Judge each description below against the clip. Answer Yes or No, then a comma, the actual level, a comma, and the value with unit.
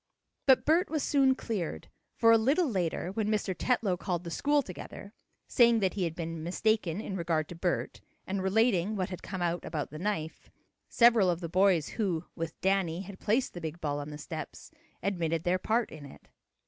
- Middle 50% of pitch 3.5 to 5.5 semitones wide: Yes, average, 4.7 semitones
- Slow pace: No, average, 200 wpm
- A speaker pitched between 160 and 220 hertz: Yes, medium, 185 Hz